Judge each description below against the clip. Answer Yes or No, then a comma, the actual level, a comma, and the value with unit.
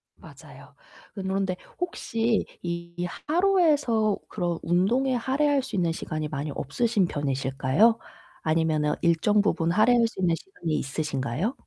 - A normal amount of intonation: No, wide, 6.7 semitones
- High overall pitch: No, medium, 180 Hz